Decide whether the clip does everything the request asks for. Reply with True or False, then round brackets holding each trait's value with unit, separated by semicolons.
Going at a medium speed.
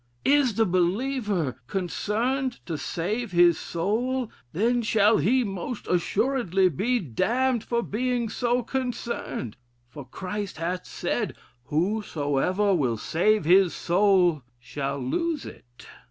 False (115 wpm)